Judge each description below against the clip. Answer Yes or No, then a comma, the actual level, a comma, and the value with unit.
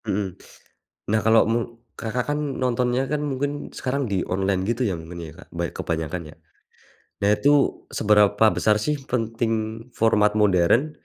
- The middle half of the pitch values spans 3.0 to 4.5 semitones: Yes, average, 4.2 semitones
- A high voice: No, low, 110 Hz